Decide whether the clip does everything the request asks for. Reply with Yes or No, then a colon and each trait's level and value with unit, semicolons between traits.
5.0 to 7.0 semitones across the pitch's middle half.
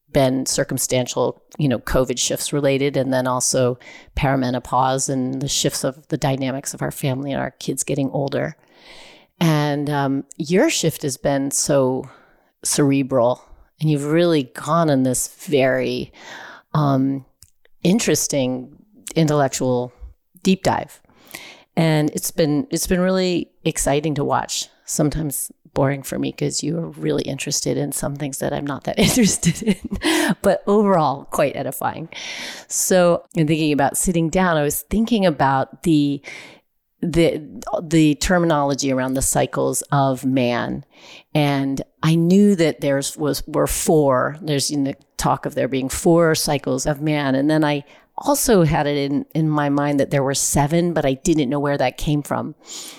No: average, 3.4 semitones